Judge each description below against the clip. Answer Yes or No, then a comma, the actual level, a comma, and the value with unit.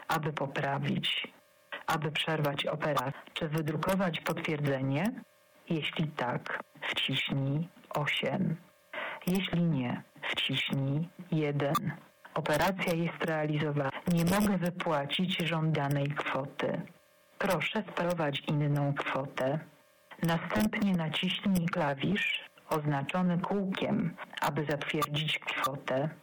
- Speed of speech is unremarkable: No, slow, 80 wpm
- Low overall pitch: No, medium, 160 Hz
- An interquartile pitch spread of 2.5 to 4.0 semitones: Yes, average, 3.6 semitones